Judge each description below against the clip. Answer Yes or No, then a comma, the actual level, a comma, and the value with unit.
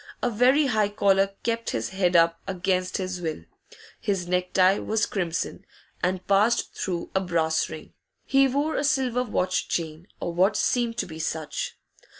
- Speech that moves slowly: No, average, 160 wpm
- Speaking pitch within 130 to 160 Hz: No, high, 190 Hz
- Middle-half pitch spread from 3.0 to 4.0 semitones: No, average, 4.7 semitones